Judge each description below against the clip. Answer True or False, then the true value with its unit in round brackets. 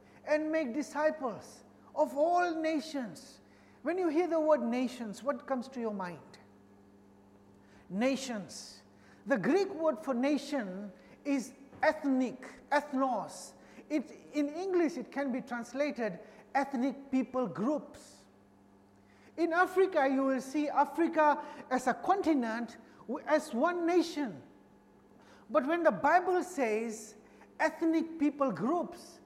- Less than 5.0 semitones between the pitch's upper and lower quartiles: False (5.4 semitones)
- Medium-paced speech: False (115 wpm)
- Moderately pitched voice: False (275 Hz)